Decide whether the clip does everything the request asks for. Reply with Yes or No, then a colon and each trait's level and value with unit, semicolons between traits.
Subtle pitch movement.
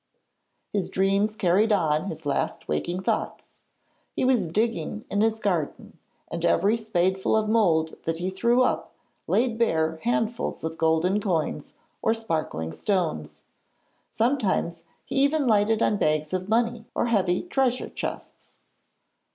No: wide, 5.4 semitones